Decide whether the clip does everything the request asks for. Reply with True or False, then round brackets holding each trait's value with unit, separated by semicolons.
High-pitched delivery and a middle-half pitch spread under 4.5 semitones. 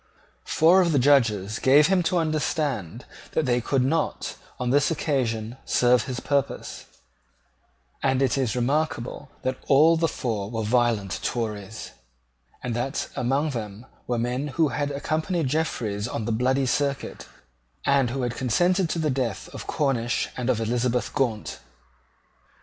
False (130 Hz; 3.7 semitones)